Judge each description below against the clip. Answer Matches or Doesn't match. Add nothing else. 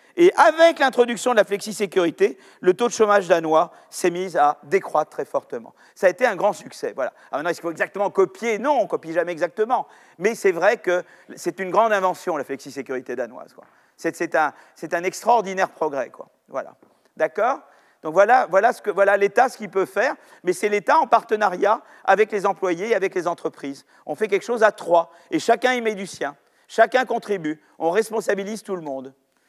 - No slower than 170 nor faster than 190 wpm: Doesn't match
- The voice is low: Doesn't match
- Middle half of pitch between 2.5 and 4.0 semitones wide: Doesn't match